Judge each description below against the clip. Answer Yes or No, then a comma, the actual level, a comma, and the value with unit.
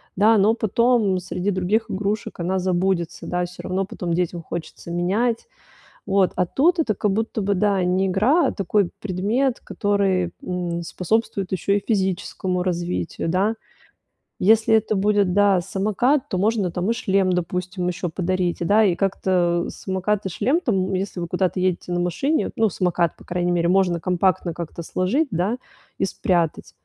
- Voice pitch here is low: No, high, 190 Hz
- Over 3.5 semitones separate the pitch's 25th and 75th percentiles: No, average, 2.8 semitones